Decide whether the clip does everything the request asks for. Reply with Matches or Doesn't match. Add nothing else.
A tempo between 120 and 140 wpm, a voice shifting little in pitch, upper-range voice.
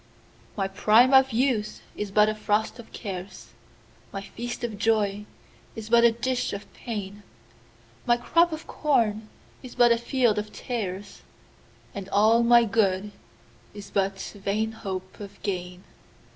Doesn't match